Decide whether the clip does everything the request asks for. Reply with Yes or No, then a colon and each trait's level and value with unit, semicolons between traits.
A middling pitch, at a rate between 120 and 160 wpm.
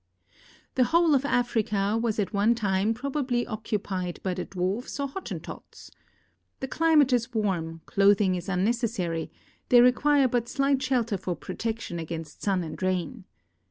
No: high, 220 Hz; average, 150 wpm